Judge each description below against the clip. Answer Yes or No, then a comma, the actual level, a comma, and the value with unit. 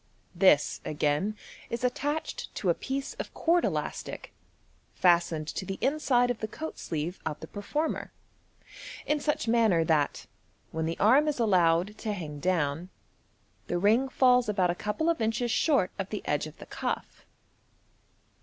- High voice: Yes, high, 210 Hz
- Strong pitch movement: Yes, wide, 6.8 semitones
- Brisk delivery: No, average, 160 wpm